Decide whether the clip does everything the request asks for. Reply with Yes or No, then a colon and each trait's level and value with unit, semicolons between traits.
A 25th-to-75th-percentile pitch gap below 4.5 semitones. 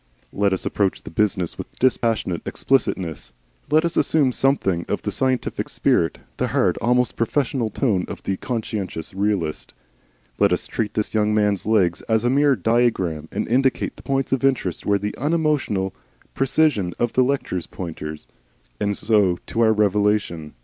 No: average, 5.3 semitones